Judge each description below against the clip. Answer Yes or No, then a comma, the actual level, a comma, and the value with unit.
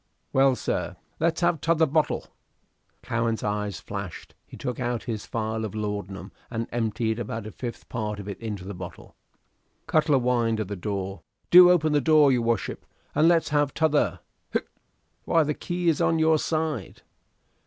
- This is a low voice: Yes, low, 120 Hz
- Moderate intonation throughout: No, wide, 6.6 semitones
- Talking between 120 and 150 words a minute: No, average, 170 wpm